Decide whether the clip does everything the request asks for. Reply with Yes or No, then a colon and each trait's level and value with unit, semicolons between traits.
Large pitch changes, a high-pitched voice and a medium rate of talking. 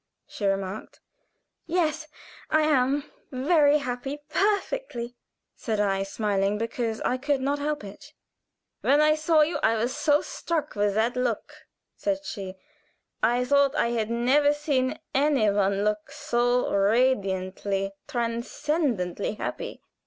No: wide, 5.8 semitones; very high, 250 Hz; slow, 130 wpm